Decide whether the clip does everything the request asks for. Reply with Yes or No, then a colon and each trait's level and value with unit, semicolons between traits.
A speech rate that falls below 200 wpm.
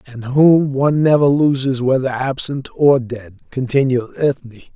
Yes: average, 140 wpm